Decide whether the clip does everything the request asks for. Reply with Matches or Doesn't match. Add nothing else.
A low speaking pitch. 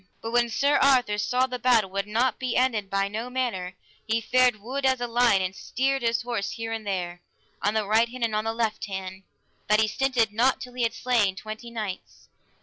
Doesn't match